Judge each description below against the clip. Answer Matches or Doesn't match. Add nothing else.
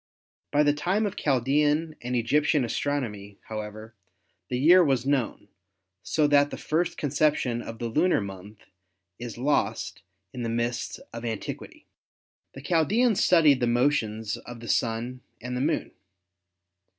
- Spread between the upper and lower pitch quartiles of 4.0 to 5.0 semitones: Matches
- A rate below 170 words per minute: Matches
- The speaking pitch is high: Doesn't match